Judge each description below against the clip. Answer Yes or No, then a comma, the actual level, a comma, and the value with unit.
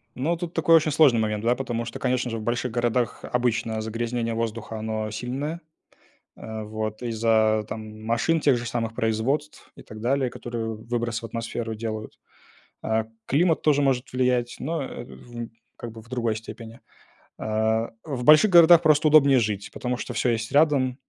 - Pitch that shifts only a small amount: No, average, 3.1 semitones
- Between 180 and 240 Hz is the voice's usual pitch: No, low, 120 Hz